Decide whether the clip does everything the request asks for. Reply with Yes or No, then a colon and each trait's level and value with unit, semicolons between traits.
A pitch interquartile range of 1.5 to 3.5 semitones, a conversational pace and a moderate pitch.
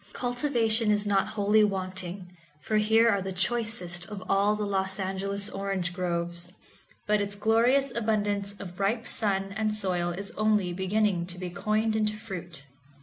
No: narrow, 2.5 semitones; average, 155 wpm; high, 200 Hz